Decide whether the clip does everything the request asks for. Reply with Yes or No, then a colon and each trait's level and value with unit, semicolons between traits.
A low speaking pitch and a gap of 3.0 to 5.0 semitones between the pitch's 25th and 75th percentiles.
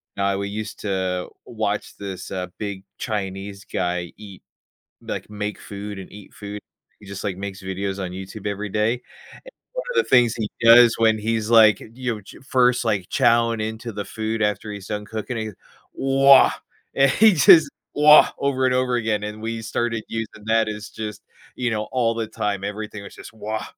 No: low, 110 Hz; narrow, 2.5 semitones